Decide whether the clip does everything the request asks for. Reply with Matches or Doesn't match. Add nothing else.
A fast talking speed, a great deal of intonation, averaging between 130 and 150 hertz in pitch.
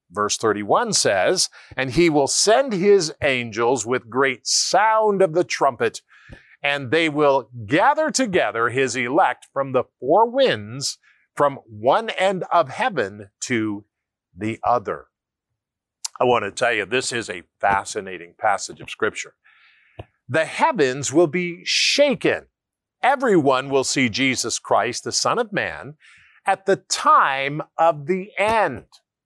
Doesn't match